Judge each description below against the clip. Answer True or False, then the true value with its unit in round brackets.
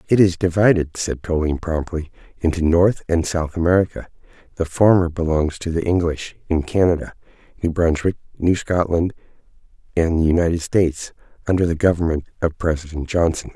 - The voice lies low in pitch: True (85 Hz)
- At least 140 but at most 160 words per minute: True (145 wpm)